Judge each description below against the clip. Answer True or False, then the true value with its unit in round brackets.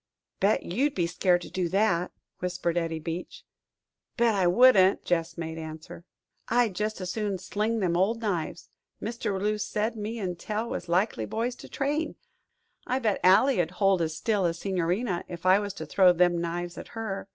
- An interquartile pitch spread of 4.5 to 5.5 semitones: False (3.8 semitones)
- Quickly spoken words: False (185 wpm)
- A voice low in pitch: False (190 Hz)